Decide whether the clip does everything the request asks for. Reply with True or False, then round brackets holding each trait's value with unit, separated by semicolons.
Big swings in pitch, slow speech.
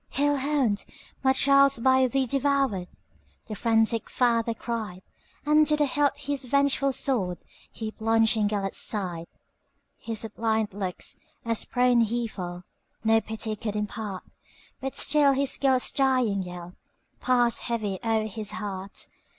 False (4.2 semitones; 120 wpm)